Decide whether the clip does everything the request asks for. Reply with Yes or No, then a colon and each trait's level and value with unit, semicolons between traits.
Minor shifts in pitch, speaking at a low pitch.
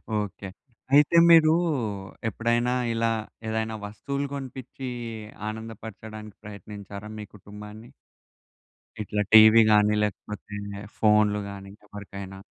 Yes: narrow, 1.8 semitones; low, 105 Hz